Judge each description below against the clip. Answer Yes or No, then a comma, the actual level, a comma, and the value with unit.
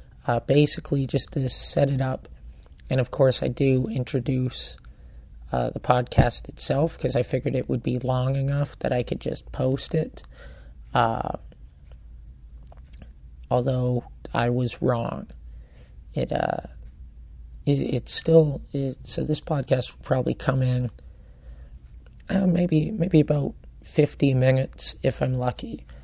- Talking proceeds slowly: Yes, slow, 130 wpm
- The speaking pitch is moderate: No, low, 125 Hz